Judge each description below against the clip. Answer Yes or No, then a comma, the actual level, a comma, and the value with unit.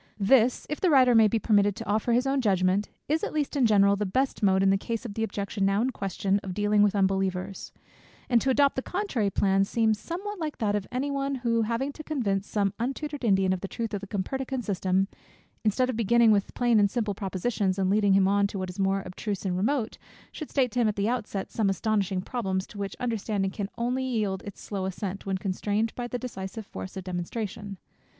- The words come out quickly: Yes, fast, 230 wpm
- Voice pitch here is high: Yes, high, 210 Hz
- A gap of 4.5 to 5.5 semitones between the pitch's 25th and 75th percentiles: No, average, 3.9 semitones